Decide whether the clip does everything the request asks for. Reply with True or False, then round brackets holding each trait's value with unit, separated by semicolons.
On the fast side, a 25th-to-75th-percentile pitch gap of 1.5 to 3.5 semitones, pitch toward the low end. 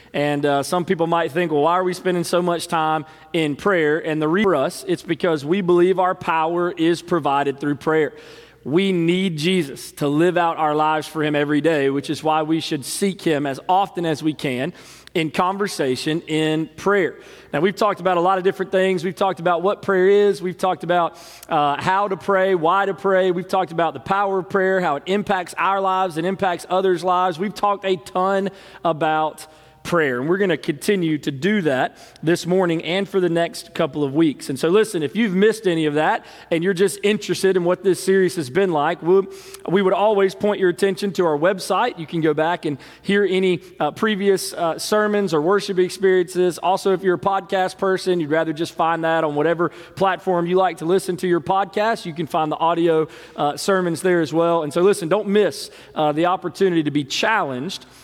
False (215 wpm; 3.0 semitones; 180 Hz)